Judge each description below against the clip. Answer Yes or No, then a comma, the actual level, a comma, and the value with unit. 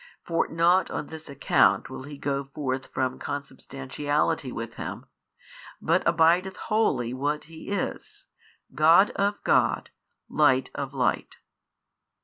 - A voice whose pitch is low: No, medium, 145 Hz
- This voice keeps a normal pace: No, slow, 125 wpm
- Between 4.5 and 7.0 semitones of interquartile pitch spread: No, average, 3.8 semitones